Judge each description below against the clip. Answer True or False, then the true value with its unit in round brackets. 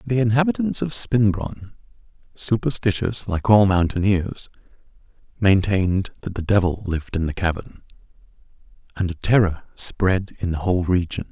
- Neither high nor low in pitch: False (100 Hz)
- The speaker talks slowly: True (125 wpm)